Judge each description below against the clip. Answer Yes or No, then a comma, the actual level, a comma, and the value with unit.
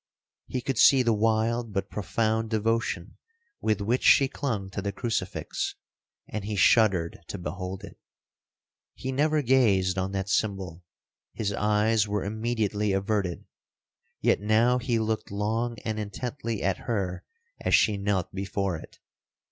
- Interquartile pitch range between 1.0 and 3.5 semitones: Yes, average, 2.9 semitones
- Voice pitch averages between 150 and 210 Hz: No, low, 105 Hz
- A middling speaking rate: No, slow, 130 wpm